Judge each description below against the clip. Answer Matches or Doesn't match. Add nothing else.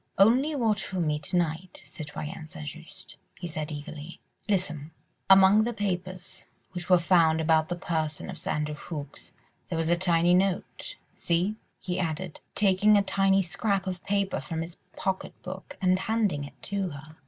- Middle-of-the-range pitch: Matches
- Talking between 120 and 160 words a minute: Doesn't match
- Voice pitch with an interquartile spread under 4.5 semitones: Matches